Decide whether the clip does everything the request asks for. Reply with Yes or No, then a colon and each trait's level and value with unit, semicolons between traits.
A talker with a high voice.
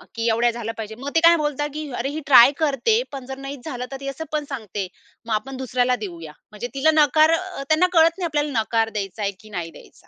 Yes: very high, 270 Hz